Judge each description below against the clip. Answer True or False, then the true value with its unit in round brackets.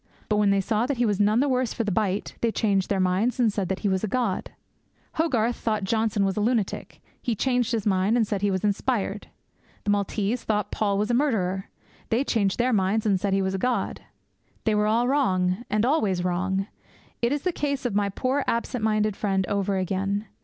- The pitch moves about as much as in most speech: True (3.4 semitones)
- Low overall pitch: False (210 Hz)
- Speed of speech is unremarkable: False (220 wpm)